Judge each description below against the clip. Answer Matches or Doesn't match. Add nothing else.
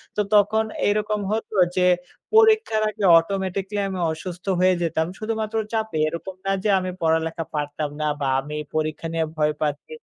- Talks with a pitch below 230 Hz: Matches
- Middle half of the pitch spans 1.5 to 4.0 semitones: Doesn't match